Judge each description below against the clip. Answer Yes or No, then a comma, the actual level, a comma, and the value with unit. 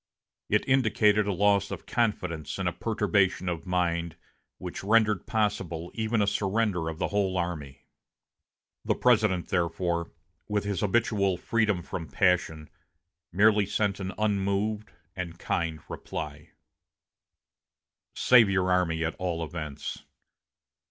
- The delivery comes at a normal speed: No, slow, 125 wpm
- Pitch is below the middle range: Yes, very low, 95 Hz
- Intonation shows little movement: No, average, 3.6 semitones